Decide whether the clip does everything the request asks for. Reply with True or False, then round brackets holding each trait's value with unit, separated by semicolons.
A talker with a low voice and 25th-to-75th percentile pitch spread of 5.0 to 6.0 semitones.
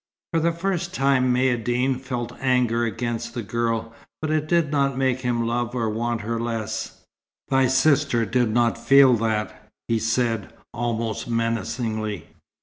False (120 Hz; 2.5 semitones)